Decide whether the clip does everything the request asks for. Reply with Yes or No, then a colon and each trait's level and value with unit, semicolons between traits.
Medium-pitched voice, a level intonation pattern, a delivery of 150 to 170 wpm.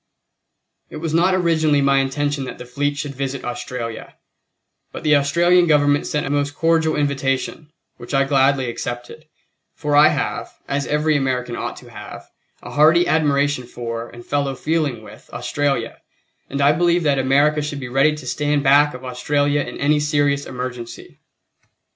Yes: medium, 145 Hz; narrow, 2.3 semitones; average, 165 wpm